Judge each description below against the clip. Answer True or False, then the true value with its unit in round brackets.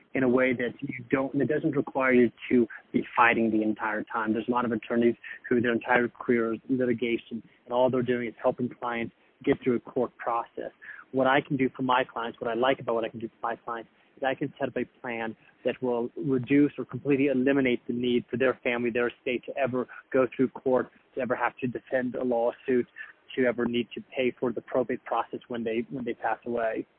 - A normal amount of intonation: False (1.7 semitones)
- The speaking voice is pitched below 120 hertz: False (125 Hz)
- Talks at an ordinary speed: False (235 wpm)